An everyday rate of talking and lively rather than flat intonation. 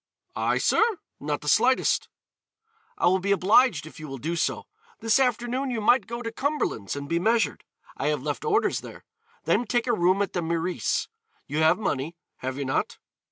Yes: average, 190 wpm; wide, 7.2 semitones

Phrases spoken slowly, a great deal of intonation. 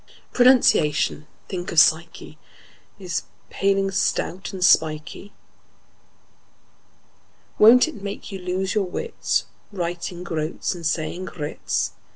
No: slow, 105 wpm; average, 3.5 semitones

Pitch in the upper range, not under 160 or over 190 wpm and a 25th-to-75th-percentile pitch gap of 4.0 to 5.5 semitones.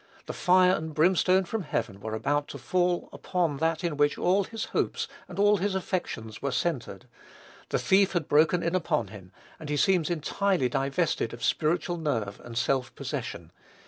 No: medium, 165 Hz; average, 175 wpm; average, 4.8 semitones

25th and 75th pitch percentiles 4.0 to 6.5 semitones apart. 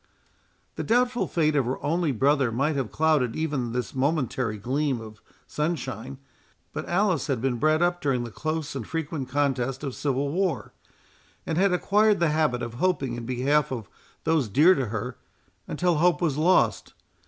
Yes: average, 4.4 semitones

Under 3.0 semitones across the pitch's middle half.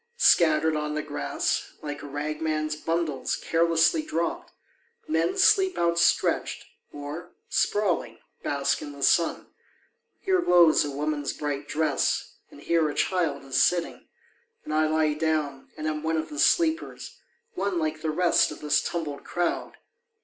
Yes: narrow, 2.5 semitones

